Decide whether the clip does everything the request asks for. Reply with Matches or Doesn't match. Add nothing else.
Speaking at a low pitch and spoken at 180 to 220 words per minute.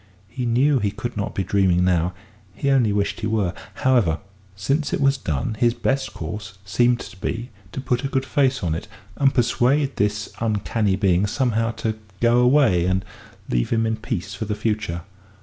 Matches